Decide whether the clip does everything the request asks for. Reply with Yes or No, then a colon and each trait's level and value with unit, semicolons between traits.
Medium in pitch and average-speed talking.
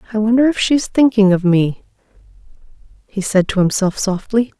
No: high, 210 Hz; average, 155 wpm